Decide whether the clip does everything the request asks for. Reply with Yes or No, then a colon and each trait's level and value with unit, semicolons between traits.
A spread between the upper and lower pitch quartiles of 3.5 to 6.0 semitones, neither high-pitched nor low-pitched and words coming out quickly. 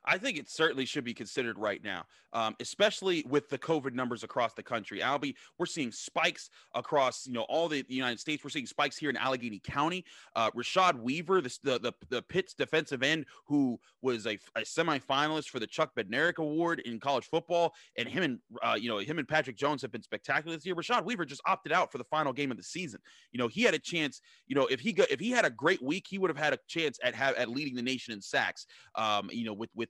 Yes: average, 4.7 semitones; medium, 145 Hz; fast, 245 wpm